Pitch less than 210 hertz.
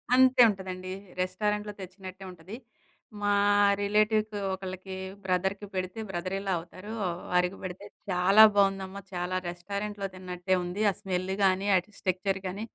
Yes: high, 190 Hz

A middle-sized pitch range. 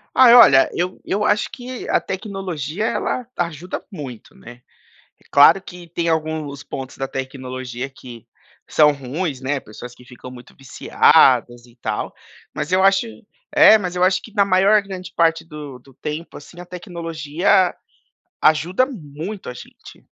No: wide, 6.0 semitones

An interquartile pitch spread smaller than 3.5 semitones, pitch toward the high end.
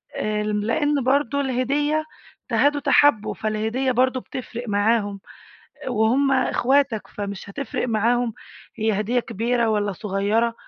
No: average, 3.8 semitones; high, 235 Hz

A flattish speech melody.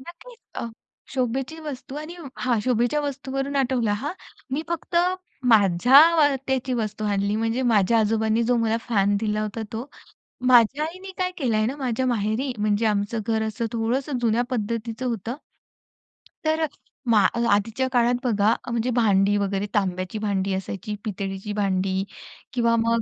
No: average, 3.9 semitones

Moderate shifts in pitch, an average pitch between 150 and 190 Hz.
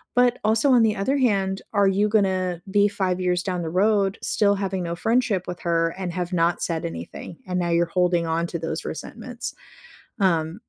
Yes: average, 3.0 semitones; medium, 185 Hz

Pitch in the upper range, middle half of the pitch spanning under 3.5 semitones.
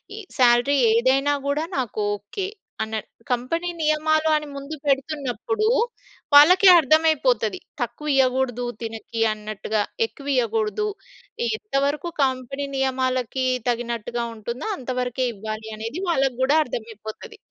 No: very high, 260 Hz; average, 4.3 semitones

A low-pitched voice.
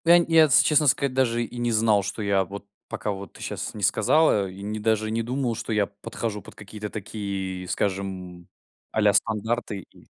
Yes: low, 105 Hz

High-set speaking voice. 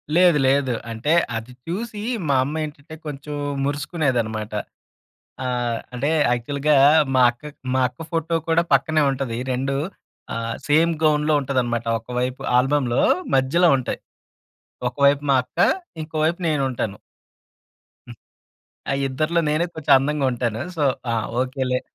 No: medium, 140 Hz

